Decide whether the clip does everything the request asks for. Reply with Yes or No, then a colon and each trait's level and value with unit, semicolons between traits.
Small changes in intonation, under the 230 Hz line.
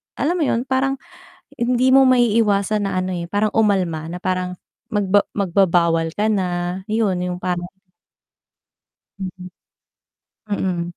No: average, 3.3 semitones; high, 190 Hz